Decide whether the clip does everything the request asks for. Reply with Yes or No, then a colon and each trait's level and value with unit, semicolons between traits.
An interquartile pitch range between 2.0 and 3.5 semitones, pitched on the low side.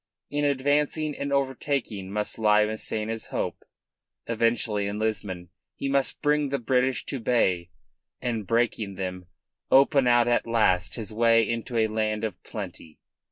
No: average, 4.0 semitones; low, 115 Hz